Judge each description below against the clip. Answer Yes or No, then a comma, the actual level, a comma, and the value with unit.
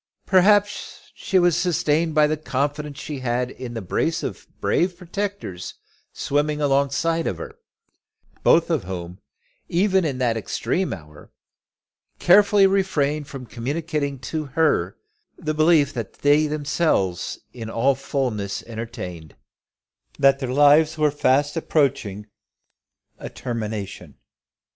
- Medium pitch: Yes, medium, 145 Hz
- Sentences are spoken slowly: Yes, slow, 125 wpm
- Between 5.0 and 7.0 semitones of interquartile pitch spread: Yes, wide, 5.5 semitones